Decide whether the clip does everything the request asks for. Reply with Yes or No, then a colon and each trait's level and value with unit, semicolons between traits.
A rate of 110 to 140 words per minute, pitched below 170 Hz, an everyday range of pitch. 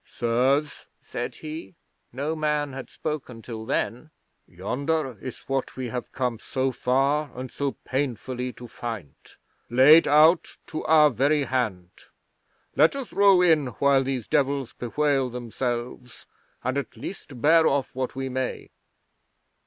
Yes: slow, 135 wpm; low, 135 Hz; average, 3.4 semitones